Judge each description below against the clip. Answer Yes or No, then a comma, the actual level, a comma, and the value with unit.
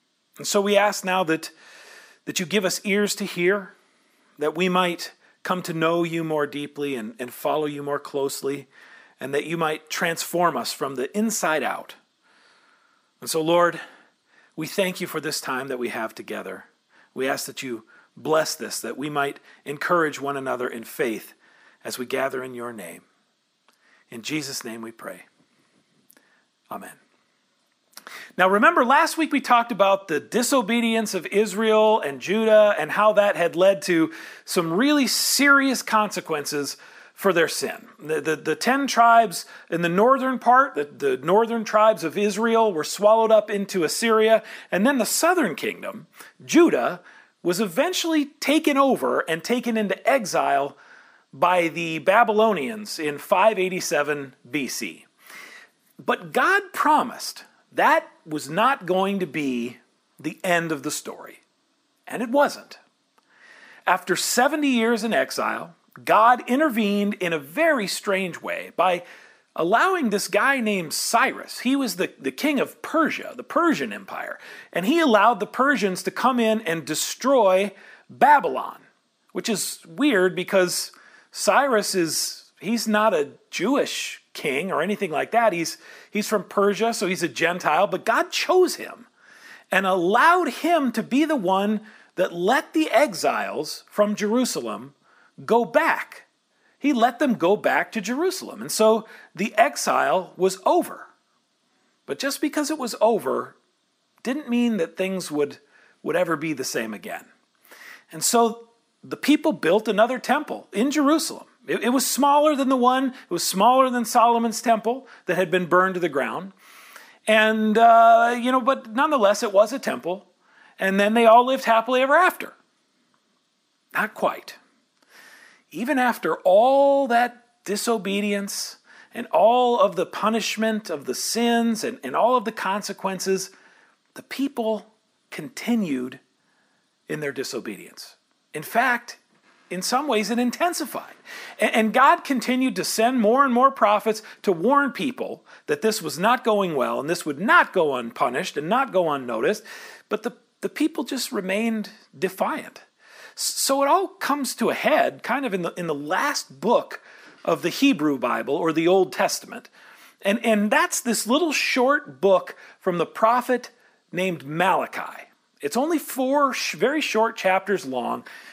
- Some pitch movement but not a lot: No, wide, 6.0 semitones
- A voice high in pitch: Yes, high, 220 Hz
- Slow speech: No, average, 155 wpm